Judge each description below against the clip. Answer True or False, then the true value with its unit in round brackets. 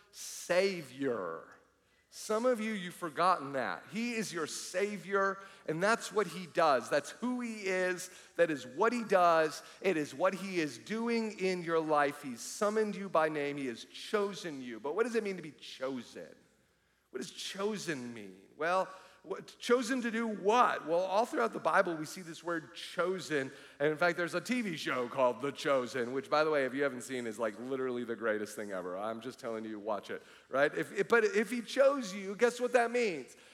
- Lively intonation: True (7.1 semitones)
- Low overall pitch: False (175 Hz)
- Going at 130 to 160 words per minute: False (205 wpm)